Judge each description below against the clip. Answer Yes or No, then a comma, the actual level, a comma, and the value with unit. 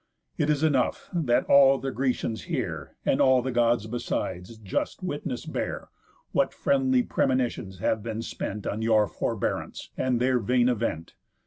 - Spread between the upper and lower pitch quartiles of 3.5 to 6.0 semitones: No, average, 2.9 semitones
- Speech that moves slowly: No, average, 150 wpm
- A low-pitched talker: Yes, low, 120 Hz